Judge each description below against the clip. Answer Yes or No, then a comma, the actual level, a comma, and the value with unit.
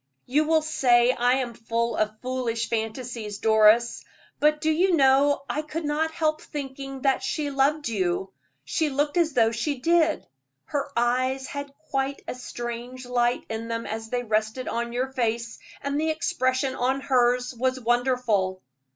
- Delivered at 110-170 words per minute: Yes, average, 160 wpm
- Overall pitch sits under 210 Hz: No, very high, 255 Hz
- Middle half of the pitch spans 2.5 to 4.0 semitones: Yes, average, 3.4 semitones